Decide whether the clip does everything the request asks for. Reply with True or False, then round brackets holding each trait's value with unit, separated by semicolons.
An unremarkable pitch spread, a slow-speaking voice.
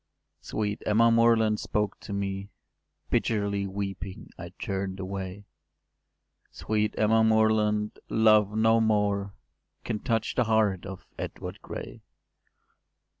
False (1.9 semitones; 115 wpm)